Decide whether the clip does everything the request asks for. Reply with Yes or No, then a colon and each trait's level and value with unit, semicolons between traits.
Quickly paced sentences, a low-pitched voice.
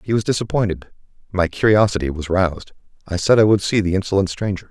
No: average, 190 wpm; very low, 95 Hz